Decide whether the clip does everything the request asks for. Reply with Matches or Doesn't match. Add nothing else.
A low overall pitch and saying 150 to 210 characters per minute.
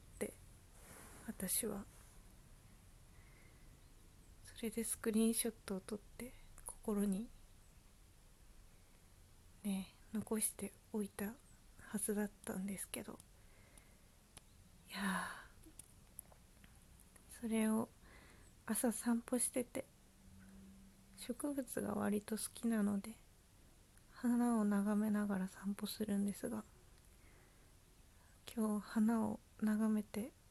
Doesn't match